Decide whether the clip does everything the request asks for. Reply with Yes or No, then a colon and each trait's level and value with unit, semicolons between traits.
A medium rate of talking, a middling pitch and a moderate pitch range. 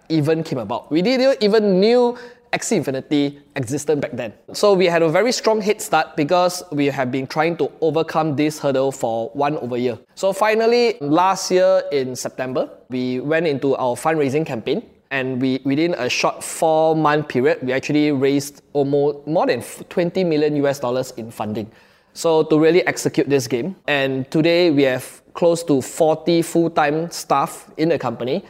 Yes: average, 175 wpm; medium, 150 Hz; average, 3.8 semitones